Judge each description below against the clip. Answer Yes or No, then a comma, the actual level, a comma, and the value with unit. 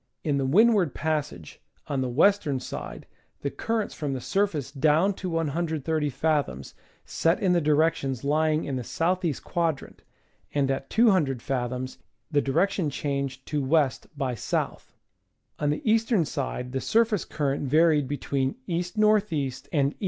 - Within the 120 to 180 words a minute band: Yes, average, 160 wpm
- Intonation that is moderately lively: Yes, average, 4.0 semitones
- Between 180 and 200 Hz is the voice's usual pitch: No, medium, 150 Hz